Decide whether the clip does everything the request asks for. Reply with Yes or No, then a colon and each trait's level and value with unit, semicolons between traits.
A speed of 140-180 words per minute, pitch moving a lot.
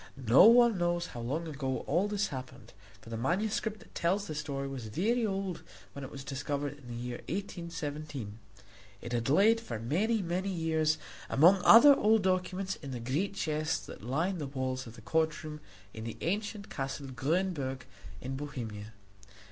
Yes: average, 170 wpm; wide, 6.4 semitones